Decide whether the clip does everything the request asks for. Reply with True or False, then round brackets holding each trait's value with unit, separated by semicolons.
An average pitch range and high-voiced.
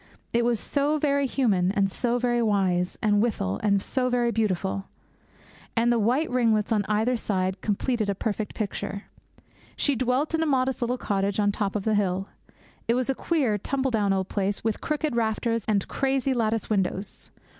True (3.9 semitones; 225 Hz)